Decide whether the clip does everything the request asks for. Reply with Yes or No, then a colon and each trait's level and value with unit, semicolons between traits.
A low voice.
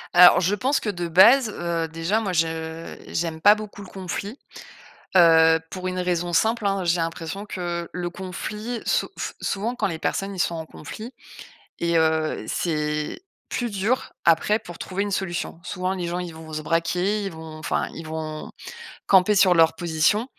No: medium, 175 Hz